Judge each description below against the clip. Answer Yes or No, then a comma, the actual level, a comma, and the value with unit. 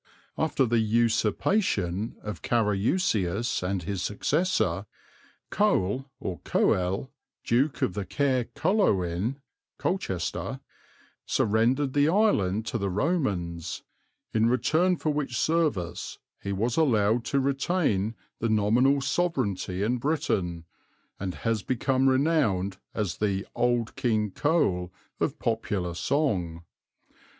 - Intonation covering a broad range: Yes, wide, 6.3 semitones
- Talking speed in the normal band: No, slow, 105 wpm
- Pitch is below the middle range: Yes, low, 115 Hz